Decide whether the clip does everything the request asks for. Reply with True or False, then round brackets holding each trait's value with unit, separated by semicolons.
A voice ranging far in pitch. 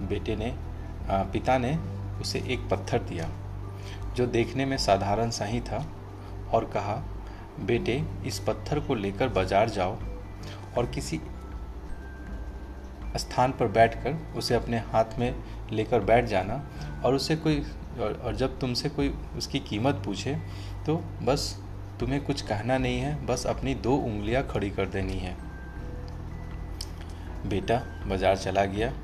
False (4.2 semitones)